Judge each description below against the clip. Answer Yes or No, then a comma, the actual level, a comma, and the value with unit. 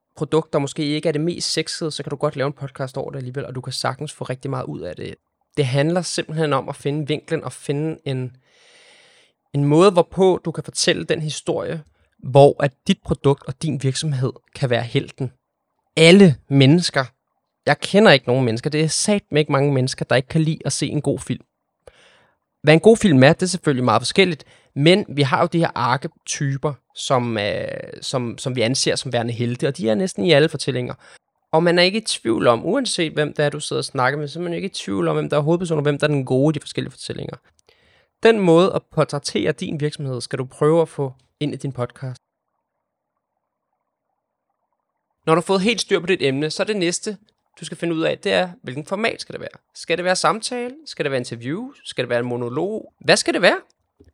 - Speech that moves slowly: No, fast, 225 wpm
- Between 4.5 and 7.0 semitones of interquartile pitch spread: No, average, 3.8 semitones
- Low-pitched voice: No, medium, 150 Hz